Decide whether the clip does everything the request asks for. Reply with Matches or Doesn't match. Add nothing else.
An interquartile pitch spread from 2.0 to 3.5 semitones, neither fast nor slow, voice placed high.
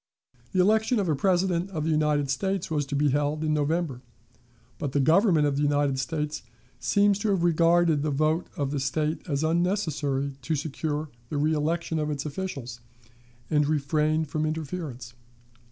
Doesn't match